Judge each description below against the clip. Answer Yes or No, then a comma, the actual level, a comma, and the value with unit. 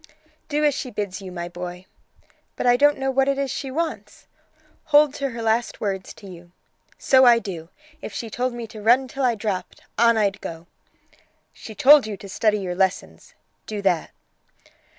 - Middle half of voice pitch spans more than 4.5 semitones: Yes, wide, 5.5 semitones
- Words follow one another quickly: No, average, 190 wpm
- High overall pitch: Yes, high, 225 Hz